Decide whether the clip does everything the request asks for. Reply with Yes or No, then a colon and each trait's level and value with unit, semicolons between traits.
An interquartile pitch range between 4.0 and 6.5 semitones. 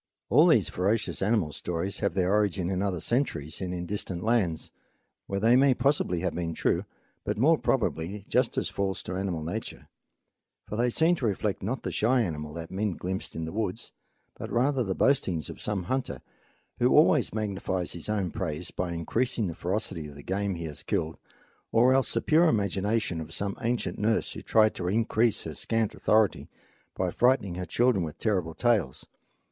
Yes: average, 4.6 semitones